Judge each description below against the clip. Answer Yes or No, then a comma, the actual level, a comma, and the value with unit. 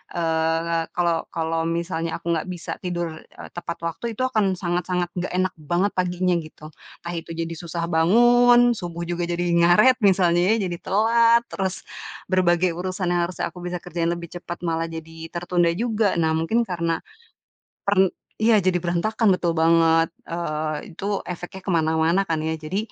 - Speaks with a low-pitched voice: No, medium, 175 Hz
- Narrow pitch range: Yes, narrow, 2.2 semitones